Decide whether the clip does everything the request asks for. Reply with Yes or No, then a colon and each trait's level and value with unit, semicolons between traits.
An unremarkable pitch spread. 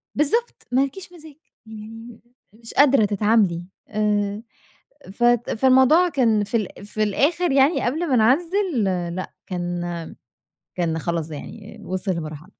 No: wide, 6.1 semitones